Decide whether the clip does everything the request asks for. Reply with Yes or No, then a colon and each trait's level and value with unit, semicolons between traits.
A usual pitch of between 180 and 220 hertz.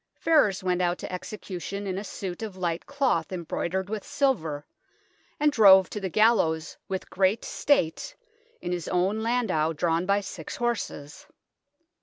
Yes: high, 190 Hz